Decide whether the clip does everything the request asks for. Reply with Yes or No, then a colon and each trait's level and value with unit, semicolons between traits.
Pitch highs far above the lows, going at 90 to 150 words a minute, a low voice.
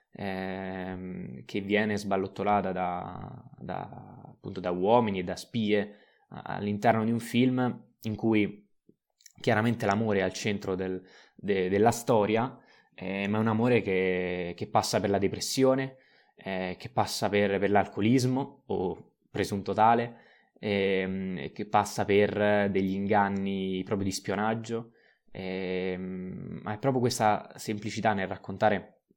No: average, 2.8 semitones; average, 130 wpm; low, 100 Hz